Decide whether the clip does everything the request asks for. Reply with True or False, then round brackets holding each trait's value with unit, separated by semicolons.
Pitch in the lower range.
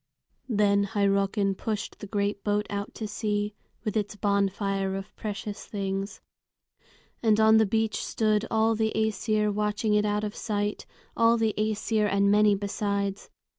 False (210 Hz)